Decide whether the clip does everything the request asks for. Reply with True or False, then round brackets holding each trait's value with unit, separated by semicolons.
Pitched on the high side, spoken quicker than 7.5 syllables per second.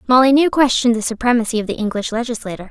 True (235 Hz; 7.8 syllables/s)